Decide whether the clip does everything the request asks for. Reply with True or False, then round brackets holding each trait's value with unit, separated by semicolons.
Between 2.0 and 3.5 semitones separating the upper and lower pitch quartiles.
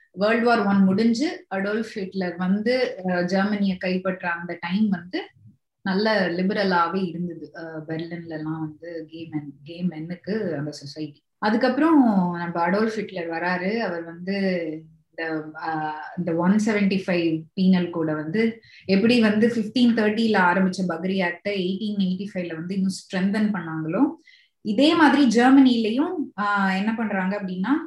False (4.1 semitones)